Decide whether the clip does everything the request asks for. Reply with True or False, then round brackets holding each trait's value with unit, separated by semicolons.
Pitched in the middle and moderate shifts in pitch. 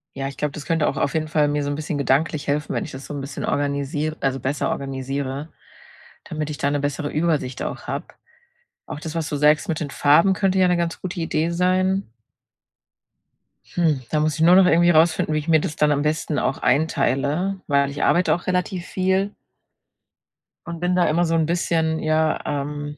True (155 Hz; 3.0 semitones)